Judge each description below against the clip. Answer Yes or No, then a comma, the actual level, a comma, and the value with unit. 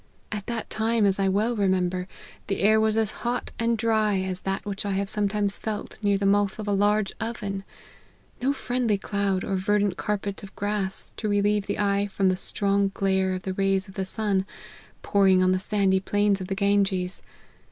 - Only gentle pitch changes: Yes, narrow, 1.5 semitones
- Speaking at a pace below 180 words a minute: No, average, 200 wpm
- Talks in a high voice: Yes, high, 200 Hz